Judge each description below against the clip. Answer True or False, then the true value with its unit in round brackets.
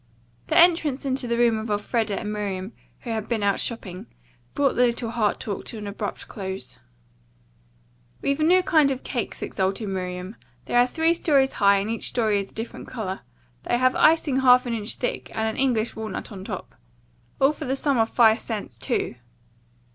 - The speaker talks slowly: False (195 wpm)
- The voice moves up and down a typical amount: True (4.2 semitones)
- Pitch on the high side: True (230 Hz)